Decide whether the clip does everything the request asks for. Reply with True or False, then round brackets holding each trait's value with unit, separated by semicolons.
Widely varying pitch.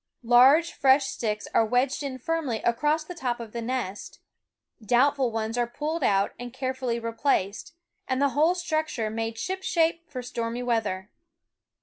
False (4.3 semitones)